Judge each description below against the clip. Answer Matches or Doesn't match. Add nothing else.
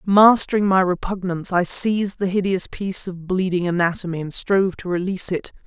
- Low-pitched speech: Doesn't match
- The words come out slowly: Doesn't match